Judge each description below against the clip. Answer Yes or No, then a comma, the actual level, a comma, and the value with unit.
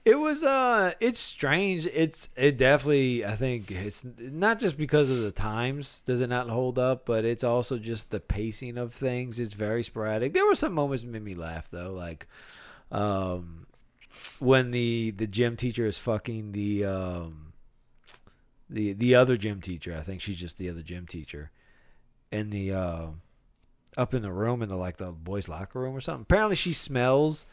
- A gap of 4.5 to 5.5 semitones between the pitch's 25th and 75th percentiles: Yes, average, 5.2 semitones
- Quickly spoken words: No, average, 185 wpm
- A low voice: Yes, low, 115 Hz